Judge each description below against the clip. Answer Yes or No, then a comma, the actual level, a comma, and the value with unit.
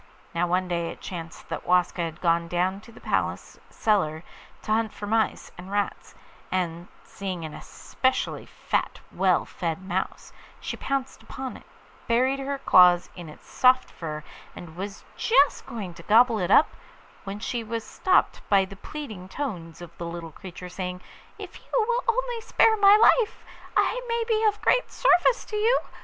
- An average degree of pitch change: No, wide, 7.7 semitones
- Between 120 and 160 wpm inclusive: No, average, 175 wpm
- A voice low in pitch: No, high, 200 Hz